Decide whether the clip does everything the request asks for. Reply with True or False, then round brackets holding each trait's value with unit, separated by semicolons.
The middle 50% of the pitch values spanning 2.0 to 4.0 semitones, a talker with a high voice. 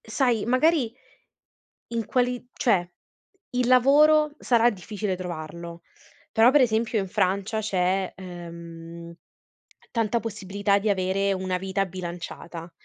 False (4.5 semitones; 200 Hz)